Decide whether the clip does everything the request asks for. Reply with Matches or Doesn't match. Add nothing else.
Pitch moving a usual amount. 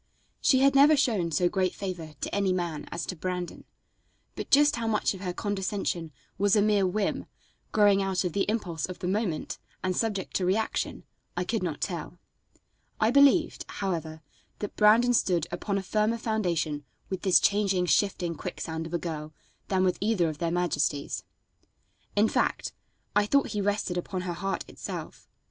Matches